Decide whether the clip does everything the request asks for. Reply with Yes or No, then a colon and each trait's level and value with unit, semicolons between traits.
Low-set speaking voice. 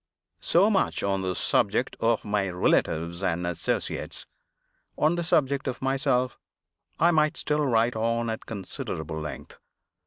Yes: low, 115 Hz